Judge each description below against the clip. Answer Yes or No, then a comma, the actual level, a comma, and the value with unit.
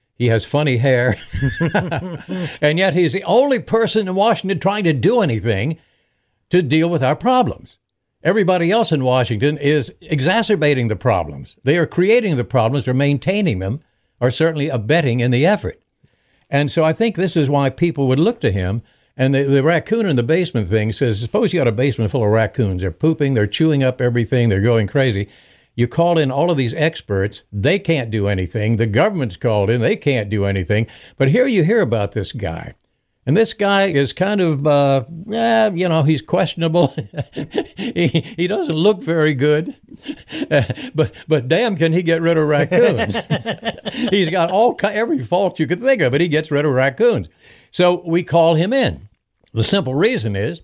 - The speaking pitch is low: No, medium, 150 Hz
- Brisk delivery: No, average, 185 wpm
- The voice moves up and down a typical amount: No, wide, 6.4 semitones